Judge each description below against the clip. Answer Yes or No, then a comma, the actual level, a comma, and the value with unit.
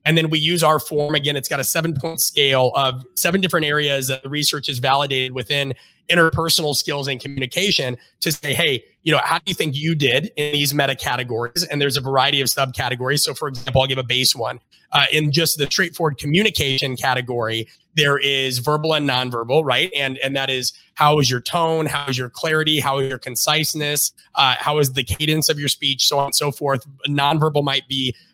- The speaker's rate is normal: No, fast, 215 wpm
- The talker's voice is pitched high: No, medium, 140 Hz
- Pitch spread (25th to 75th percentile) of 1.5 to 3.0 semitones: Yes, average, 2.7 semitones